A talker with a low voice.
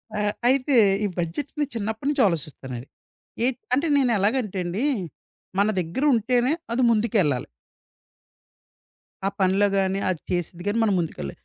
No: high, 205 Hz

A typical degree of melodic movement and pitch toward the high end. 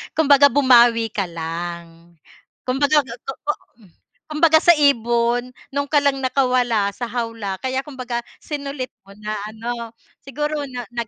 Yes: average, 3.7 semitones; very high, 250 Hz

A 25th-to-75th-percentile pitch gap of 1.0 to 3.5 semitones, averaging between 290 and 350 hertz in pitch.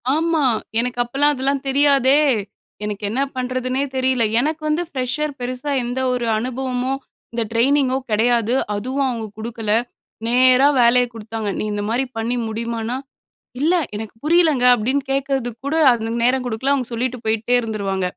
No: average, 2.8 semitones; very high, 250 Hz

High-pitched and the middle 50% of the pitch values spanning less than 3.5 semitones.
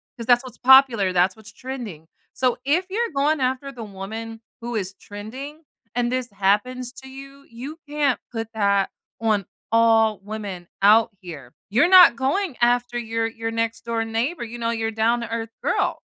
Yes: high, 230 Hz; average, 3.1 semitones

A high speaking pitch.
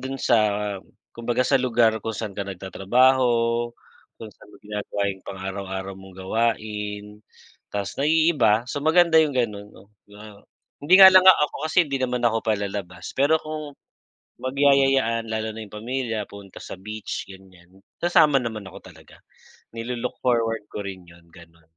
No: low, 110 Hz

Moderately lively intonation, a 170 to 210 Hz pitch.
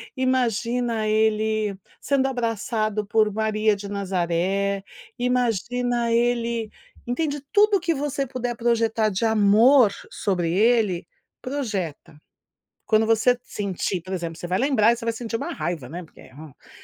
No: average, 3.6 semitones; high, 220 Hz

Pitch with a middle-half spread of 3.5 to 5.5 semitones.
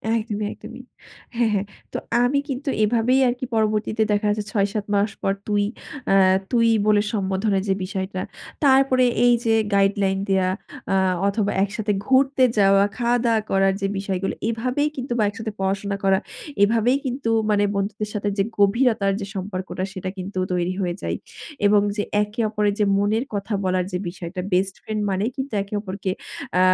No: average, 2.8 semitones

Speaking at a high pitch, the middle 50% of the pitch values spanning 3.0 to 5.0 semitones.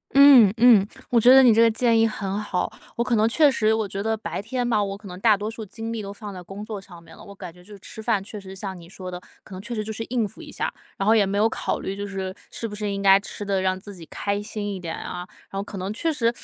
No: high, 205 Hz; narrow, 2.6 semitones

